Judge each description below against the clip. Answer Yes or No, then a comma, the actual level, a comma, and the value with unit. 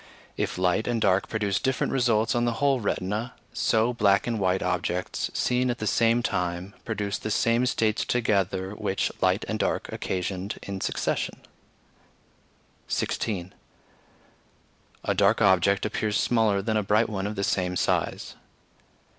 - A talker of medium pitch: No, low, 105 Hz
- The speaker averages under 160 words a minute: Yes, average, 145 wpm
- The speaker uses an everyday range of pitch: Yes, average, 3.2 semitones